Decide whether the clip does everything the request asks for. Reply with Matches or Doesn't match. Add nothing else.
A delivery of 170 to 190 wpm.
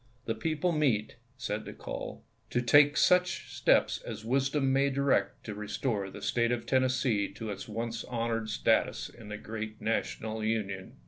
Matches